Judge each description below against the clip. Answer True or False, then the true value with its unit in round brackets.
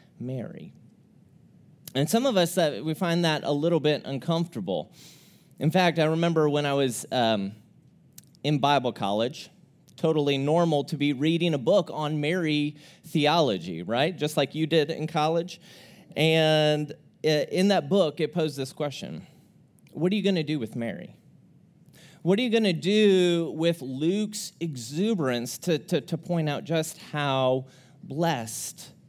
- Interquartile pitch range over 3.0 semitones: False (2.6 semitones)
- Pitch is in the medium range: True (155 Hz)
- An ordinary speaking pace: True (155 wpm)